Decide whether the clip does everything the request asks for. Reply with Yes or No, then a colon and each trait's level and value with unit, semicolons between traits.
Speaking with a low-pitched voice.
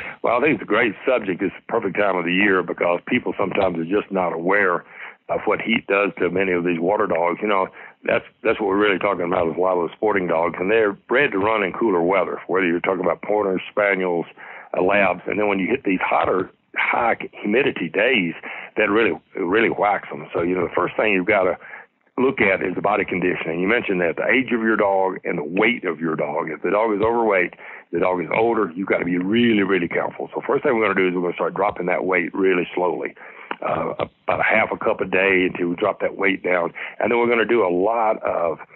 Yes: very low, 95 Hz